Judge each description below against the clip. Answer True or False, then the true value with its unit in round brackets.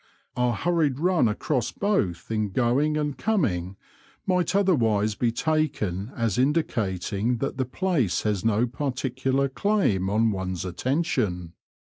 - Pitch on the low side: True (125 Hz)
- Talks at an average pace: False (130 wpm)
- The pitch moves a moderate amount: False (6.8 semitones)